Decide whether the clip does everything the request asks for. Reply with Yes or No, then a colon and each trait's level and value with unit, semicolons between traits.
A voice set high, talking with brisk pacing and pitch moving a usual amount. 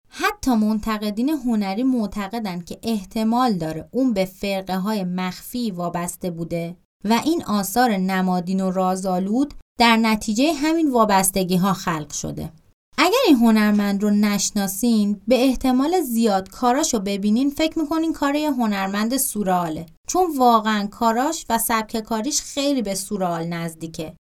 No: high, 215 Hz; average, 135 wpm; average, 4.9 semitones